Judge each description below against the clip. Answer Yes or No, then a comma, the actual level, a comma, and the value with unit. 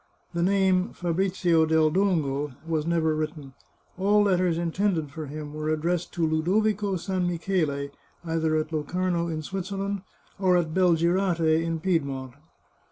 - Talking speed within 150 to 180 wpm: Yes, average, 155 wpm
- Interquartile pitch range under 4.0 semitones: Yes, average, 2.9 semitones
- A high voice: No, medium, 170 Hz